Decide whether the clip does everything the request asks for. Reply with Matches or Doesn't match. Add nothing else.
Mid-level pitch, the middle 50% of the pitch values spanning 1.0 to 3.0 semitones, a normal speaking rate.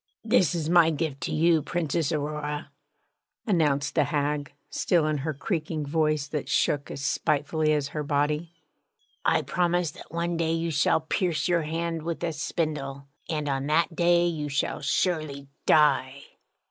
Matches